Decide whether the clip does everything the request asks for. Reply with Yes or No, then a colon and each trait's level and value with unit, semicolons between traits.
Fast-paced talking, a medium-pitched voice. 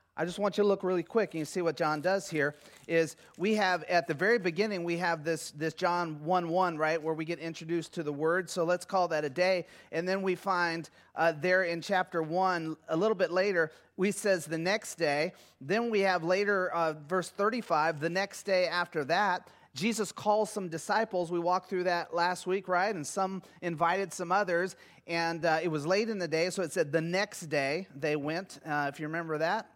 Yes: fast, 220 wpm; medium, 175 Hz